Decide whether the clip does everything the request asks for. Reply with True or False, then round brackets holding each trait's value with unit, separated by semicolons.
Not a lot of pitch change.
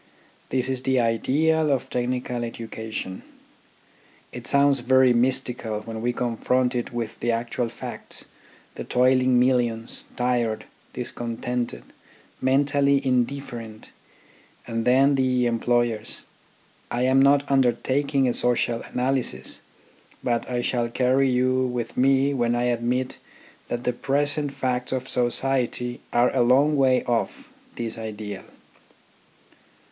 True (1.8 semitones)